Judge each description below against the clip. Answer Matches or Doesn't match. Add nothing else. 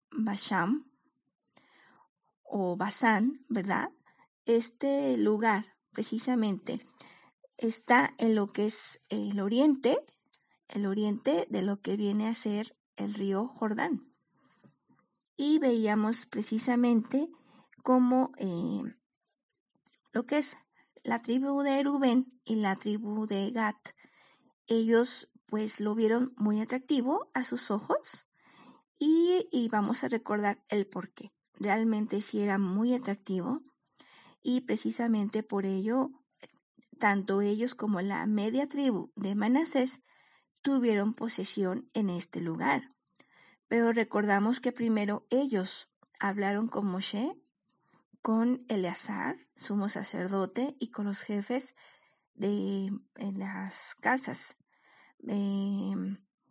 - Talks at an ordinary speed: Doesn't match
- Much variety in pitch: Doesn't match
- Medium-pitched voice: Doesn't match